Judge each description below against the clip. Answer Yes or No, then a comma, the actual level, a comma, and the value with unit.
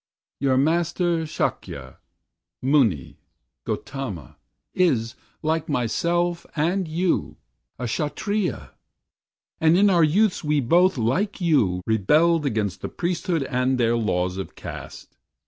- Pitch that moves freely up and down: Yes, wide, 6.7 semitones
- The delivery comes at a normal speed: No, slow, 110 wpm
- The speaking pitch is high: No, medium, 150 Hz